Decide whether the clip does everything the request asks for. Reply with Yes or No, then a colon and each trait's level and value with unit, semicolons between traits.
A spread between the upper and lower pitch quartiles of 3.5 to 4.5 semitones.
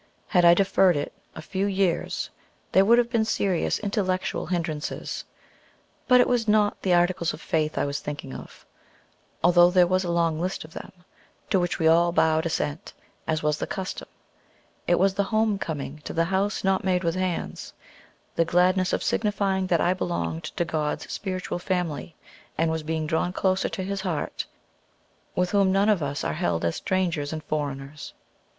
No: average, 3.1 semitones